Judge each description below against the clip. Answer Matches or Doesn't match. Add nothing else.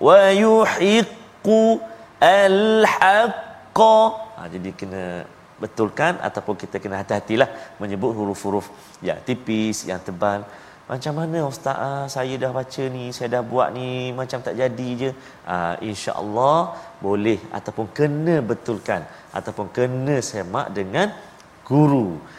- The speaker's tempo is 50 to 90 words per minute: Doesn't match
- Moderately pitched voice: Doesn't match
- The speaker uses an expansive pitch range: Matches